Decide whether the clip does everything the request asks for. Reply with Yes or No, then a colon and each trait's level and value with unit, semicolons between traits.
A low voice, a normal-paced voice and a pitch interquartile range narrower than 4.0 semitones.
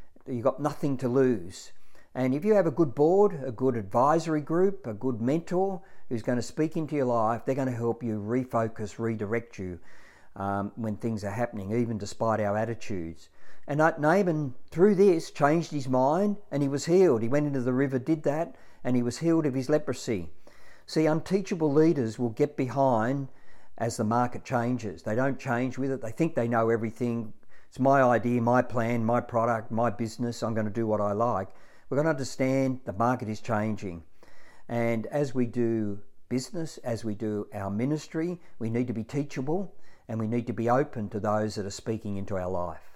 No: low, 120 Hz; average, 195 wpm; average, 4.4 semitones